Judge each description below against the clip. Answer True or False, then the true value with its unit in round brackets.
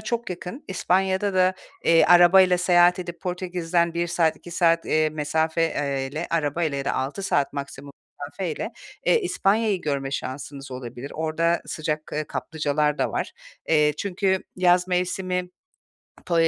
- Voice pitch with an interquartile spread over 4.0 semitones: False (3.4 semitones)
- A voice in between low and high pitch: True (170 Hz)